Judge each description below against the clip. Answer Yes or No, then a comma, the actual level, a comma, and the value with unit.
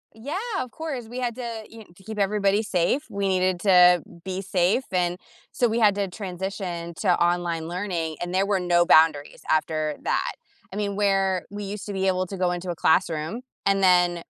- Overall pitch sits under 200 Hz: Yes, high, 190 Hz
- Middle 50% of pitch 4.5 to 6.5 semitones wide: No, average, 2.8 semitones